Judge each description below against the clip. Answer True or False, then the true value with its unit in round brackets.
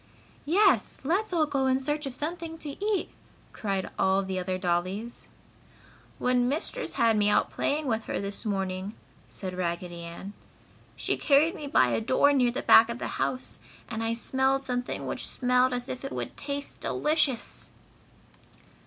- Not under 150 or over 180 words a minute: True (165 wpm)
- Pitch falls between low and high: False (245 Hz)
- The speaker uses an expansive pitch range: True (6.7 semitones)